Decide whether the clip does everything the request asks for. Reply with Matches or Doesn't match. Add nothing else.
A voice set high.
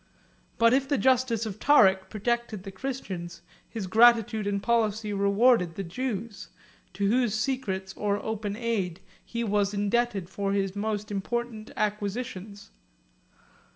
Matches